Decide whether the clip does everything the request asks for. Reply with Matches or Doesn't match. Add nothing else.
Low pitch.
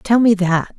Doesn't match